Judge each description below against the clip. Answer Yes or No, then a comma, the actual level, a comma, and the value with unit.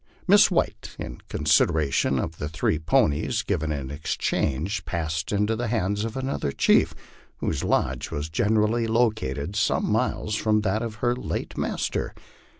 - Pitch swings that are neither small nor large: No, wide, 6.2 semitones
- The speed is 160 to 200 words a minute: No, average, 145 wpm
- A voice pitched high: No, low, 100 Hz